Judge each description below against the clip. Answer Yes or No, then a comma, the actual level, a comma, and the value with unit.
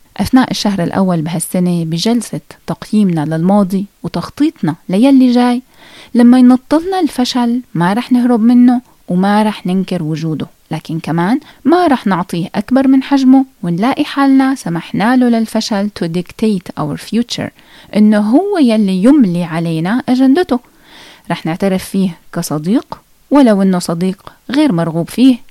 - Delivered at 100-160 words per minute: Yes, average, 125 wpm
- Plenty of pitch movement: Yes, wide, 6.4 semitones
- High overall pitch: Yes, high, 220 Hz